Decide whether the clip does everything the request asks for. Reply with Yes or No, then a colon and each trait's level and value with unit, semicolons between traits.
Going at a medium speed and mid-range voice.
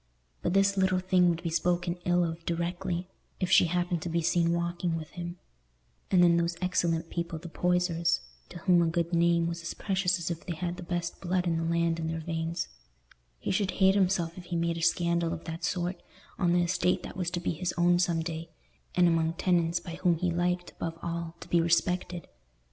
No: fast, 215 wpm; medium, 170 Hz